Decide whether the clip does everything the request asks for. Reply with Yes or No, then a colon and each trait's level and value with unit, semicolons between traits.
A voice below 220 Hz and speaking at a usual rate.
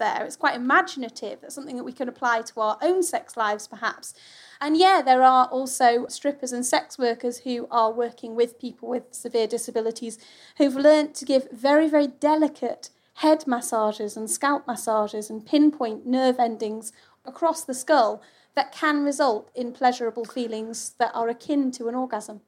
No: high, 245 Hz; average, 170 wpm